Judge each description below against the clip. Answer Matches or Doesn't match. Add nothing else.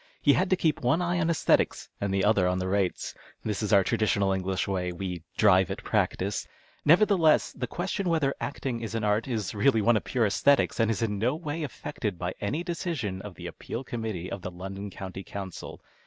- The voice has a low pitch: Matches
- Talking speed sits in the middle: Doesn't match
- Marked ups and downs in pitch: Matches